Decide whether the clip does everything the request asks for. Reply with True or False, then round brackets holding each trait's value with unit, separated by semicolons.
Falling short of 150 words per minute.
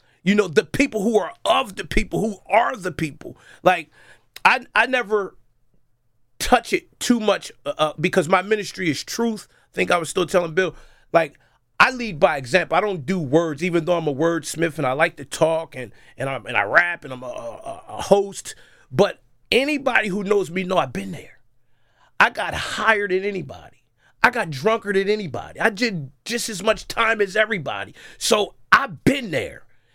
False (190 wpm)